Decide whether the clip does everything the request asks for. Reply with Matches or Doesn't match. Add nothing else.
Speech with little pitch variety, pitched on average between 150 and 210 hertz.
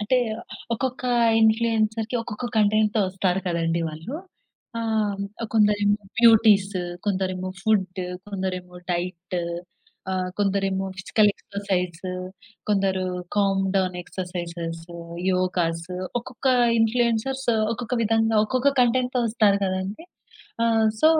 Doesn't match